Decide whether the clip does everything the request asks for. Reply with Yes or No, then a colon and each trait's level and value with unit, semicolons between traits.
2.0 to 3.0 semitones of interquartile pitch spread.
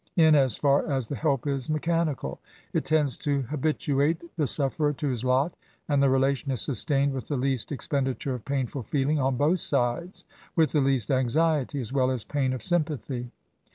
Yes: narrow, 2.6 semitones